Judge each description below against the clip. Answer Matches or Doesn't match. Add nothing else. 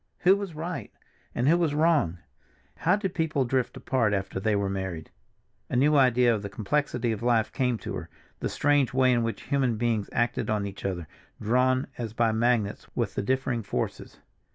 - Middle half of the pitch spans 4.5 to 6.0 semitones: Matches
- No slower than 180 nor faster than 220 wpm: Matches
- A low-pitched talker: Matches